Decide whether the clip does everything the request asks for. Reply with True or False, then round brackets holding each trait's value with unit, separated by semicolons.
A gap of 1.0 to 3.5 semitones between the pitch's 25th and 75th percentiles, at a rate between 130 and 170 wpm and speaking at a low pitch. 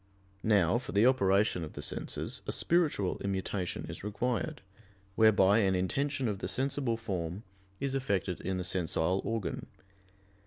False (4.3 semitones; 145 wpm; 100 Hz)